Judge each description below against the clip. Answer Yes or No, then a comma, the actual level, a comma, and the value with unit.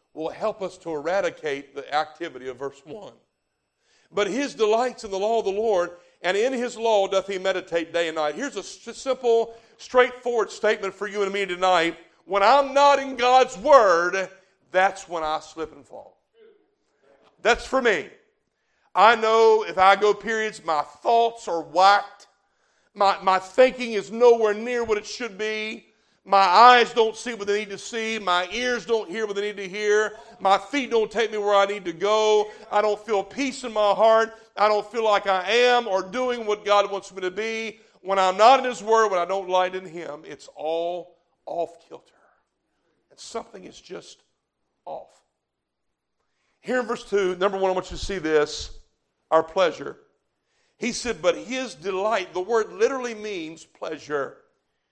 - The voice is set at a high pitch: Yes, high, 210 Hz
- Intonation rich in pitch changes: No, average, 3.7 semitones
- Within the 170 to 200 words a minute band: Yes, average, 185 wpm